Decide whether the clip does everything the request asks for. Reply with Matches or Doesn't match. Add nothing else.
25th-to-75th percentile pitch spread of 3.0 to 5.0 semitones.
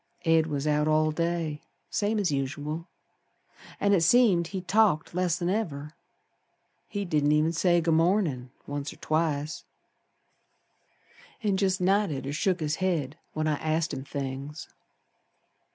Matches